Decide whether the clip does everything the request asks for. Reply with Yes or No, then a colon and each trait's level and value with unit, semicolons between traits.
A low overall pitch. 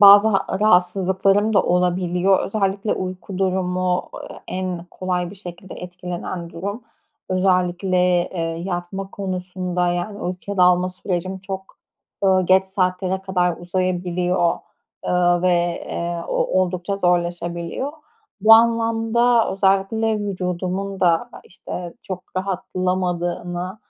No: medium, 185 Hz